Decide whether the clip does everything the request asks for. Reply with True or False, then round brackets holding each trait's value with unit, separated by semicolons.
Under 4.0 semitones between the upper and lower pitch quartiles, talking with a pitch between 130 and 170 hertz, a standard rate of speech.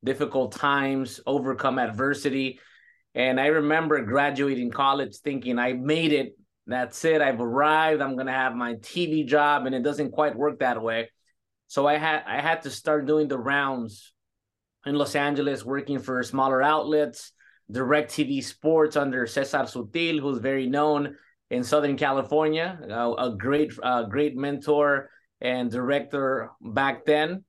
True (2.6 semitones; 140 Hz; 150 wpm)